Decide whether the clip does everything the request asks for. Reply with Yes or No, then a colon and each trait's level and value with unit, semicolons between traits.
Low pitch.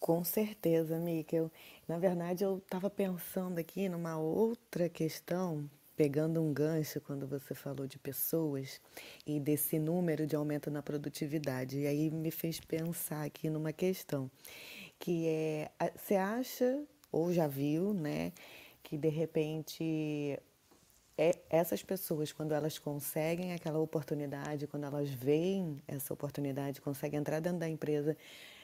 No: medium, 155 Hz